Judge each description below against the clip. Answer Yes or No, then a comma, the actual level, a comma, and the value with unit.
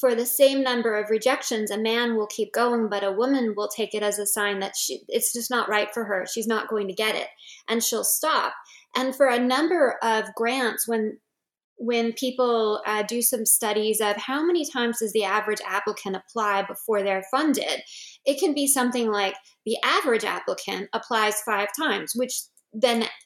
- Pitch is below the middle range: No, high, 225 Hz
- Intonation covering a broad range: No, average, 3.1 semitones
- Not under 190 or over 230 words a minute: Yes, average, 195 wpm